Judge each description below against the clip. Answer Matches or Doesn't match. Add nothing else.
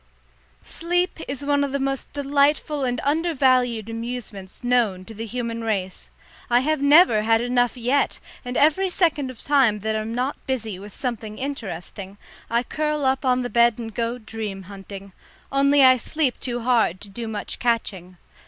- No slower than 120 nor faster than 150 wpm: Doesn't match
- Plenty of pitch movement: Doesn't match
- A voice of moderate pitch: Doesn't match